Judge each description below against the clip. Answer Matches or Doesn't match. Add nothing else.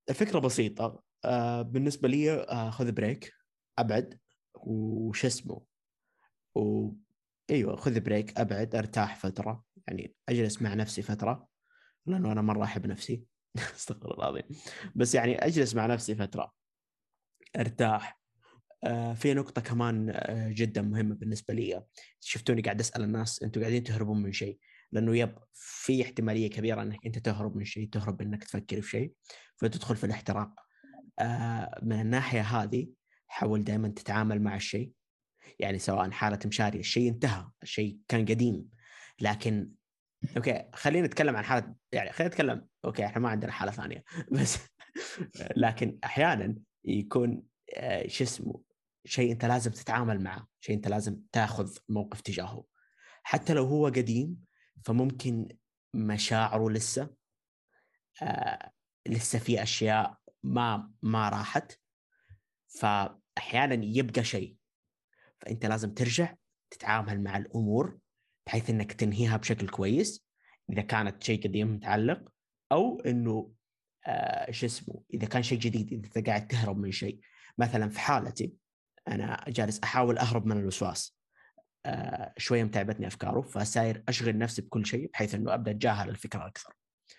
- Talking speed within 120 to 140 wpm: Matches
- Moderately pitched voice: Doesn't match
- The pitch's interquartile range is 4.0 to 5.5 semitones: Doesn't match